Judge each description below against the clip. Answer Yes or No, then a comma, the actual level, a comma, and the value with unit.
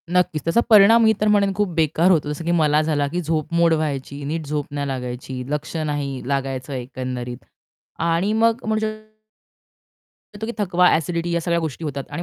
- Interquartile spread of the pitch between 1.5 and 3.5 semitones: No, average, 4.2 semitones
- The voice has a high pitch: No, medium, 160 Hz